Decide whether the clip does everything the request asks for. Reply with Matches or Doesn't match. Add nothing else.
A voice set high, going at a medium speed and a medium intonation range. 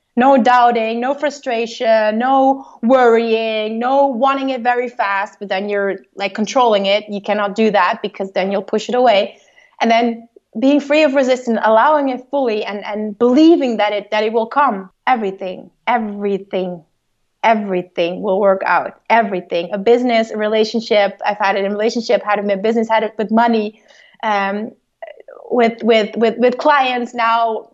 Matches